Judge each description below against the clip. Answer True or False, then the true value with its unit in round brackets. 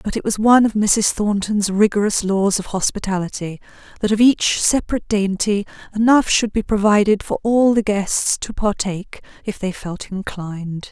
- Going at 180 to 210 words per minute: False (165 wpm)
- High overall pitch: True (205 Hz)